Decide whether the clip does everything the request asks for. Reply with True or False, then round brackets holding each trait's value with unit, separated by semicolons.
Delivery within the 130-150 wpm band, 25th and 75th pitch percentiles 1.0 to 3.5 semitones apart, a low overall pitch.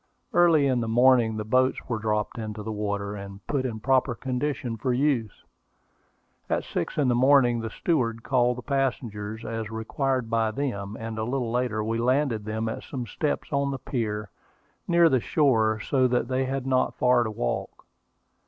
False (180 wpm; 3.2 semitones; 120 Hz)